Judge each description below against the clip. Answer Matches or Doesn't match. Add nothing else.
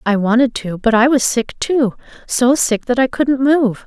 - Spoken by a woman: Matches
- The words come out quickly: Matches